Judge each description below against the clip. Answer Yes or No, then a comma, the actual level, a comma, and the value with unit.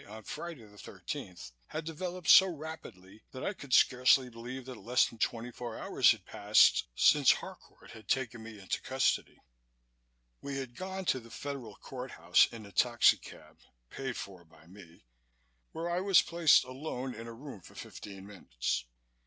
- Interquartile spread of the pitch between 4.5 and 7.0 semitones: Yes, average, 5.2 semitones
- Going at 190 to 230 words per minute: No, average, 170 wpm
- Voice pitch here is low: Yes, low, 125 Hz